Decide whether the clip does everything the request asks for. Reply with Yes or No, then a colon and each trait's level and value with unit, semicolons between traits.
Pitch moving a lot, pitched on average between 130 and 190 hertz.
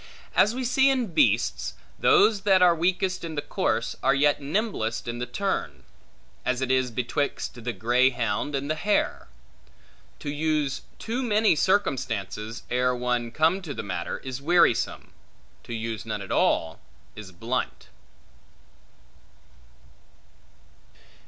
Yes: wide, 7.8 semitones; medium, 140 Hz